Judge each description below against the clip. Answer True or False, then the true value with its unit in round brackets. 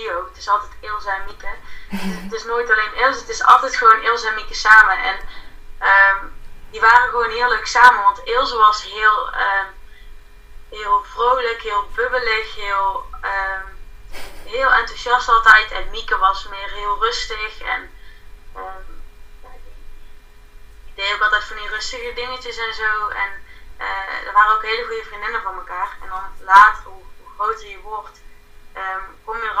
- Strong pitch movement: False (3.6 semitones)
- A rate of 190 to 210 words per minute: False (170 wpm)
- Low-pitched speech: False (215 Hz)